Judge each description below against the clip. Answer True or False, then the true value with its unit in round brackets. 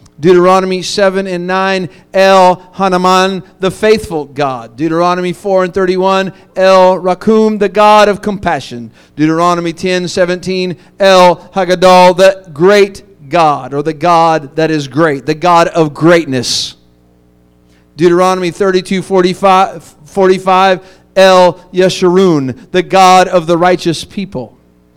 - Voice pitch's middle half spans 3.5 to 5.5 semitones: False (2.8 semitones)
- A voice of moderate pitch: True (180 Hz)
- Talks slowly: True (120 wpm)